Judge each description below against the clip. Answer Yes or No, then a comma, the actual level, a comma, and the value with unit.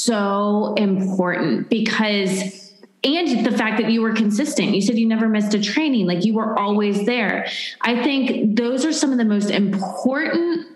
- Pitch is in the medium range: No, high, 220 Hz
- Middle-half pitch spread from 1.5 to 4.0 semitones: Yes, average, 3.4 semitones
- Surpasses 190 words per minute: No, average, 175 wpm